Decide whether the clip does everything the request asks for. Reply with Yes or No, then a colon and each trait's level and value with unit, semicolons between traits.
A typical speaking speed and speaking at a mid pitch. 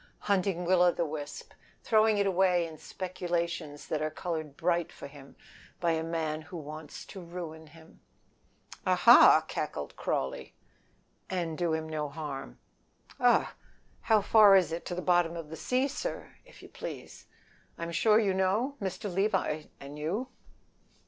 Yes: average, 155 wpm; medium, 170 Hz